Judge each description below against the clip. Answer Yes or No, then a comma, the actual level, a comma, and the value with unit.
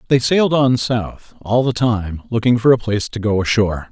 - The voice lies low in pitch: Yes, low, 115 Hz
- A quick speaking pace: Yes, fast, 215 wpm